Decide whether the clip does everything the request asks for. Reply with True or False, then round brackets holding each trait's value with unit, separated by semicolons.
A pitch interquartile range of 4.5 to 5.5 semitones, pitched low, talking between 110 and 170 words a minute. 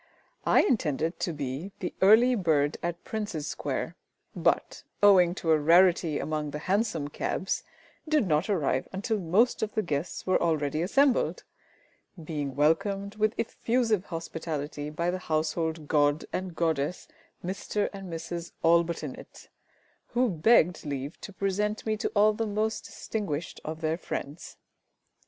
False (4.8 semitones; 170 Hz; 140 wpm)